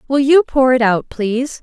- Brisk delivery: Yes, fast, 220 wpm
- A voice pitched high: Yes, very high, 255 Hz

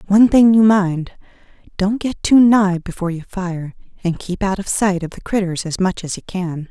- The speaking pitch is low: No, high, 190 Hz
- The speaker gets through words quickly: Yes, fast, 215 wpm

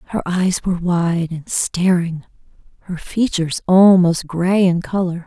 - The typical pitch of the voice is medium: Yes, medium, 175 Hz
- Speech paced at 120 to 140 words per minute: Yes, slow, 135 wpm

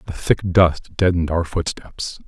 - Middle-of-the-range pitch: No, very low, 85 Hz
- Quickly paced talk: No, average, 160 wpm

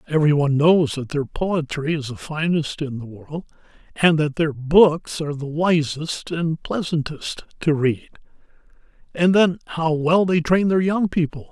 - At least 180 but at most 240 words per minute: No, average, 165 wpm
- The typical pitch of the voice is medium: Yes, medium, 155 Hz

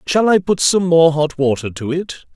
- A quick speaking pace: Yes, fast, 230 wpm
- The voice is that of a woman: No, male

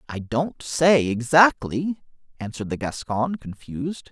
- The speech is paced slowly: Yes, slow, 115 wpm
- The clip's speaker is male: Yes, male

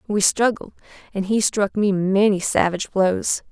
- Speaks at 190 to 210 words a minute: No, average, 155 wpm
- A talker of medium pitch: No, high, 200 Hz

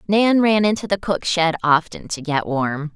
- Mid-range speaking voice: Yes, medium, 175 Hz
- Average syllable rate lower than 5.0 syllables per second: Yes, 4.4 syllables/s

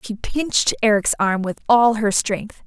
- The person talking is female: Yes, female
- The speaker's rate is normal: Yes, average, 180 wpm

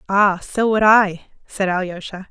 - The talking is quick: No, average, 155 wpm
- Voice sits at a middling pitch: No, high, 195 Hz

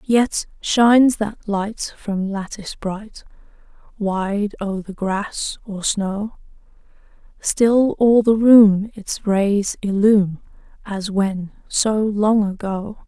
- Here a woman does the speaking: Yes, female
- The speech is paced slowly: Yes, slow, 115 wpm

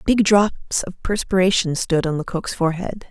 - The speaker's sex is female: Yes, female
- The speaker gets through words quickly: No, average, 155 wpm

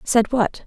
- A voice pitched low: No, high, 230 Hz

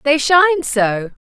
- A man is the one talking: No, female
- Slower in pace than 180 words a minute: Yes, average, 140 wpm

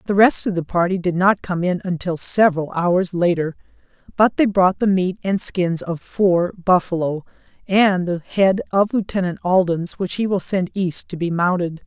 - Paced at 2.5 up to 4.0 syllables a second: No, 4.6 syllables/s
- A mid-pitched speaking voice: Yes, medium, 180 Hz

